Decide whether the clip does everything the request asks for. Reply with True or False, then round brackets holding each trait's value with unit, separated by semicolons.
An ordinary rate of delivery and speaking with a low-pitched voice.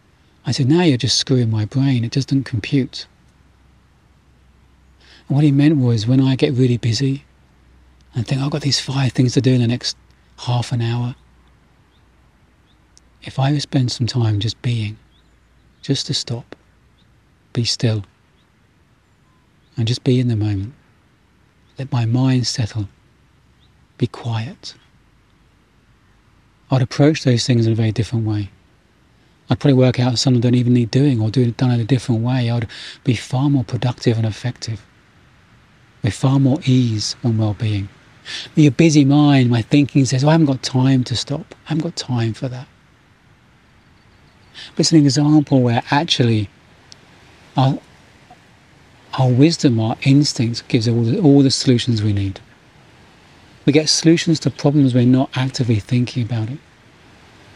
True (160 wpm; 125 Hz)